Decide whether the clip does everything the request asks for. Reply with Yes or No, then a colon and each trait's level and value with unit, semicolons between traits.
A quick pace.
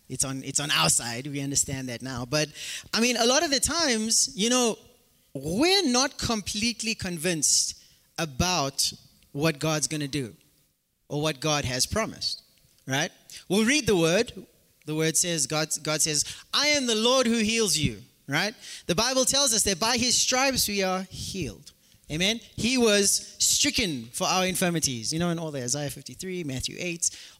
No: average, 175 wpm